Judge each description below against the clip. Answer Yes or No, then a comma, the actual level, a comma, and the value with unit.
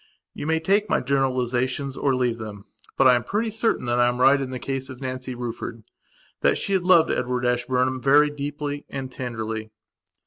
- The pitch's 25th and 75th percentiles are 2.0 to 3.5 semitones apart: Yes, average, 2.8 semitones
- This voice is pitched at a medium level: No, low, 130 Hz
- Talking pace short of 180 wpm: No, average, 185 wpm